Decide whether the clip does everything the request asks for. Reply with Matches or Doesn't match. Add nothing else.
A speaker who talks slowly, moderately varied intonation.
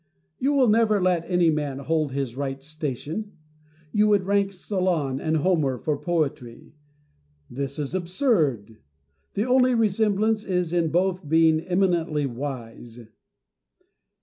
Doesn't match